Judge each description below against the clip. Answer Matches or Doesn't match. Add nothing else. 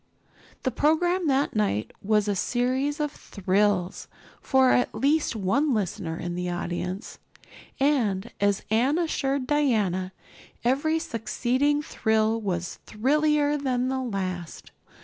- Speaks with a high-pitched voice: Matches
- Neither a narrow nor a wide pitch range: Doesn't match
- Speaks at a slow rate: Matches